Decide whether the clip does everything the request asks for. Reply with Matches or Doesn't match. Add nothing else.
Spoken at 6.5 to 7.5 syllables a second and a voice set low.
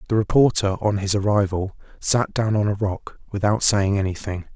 Doesn't match